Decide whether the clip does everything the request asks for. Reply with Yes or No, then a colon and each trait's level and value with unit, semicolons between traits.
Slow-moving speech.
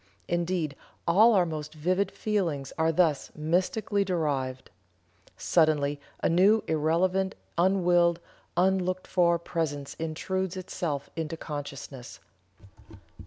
Yes: slow, 100 wpm